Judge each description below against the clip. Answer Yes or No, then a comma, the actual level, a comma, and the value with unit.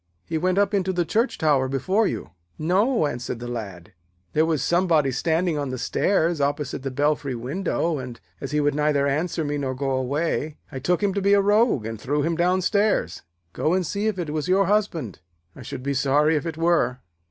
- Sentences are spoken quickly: Yes, fast, 210 wpm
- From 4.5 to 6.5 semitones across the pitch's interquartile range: Yes, average, 5.0 semitones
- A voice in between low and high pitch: Yes, medium, 155 Hz